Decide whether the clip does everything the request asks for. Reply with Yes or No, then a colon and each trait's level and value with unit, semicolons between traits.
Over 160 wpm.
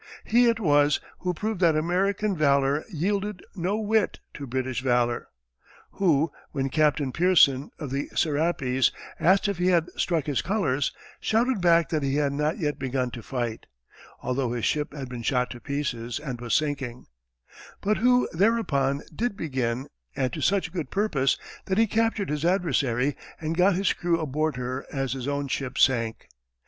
Yes: average, 170 wpm